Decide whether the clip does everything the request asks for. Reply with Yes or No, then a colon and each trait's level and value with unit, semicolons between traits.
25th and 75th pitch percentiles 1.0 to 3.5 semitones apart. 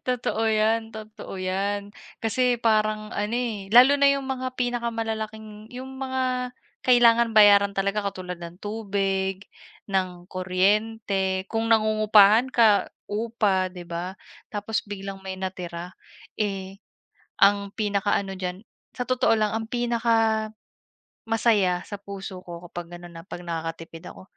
Yes: average, 3.0 semitones